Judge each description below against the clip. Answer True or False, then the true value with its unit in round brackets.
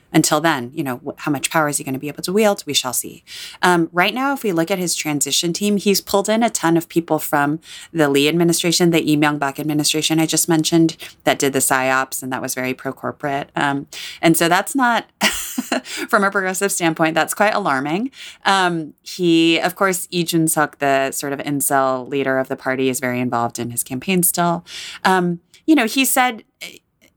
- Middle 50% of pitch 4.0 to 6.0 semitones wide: True (4.6 semitones)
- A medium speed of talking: False (210 wpm)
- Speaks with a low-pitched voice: False (160 Hz)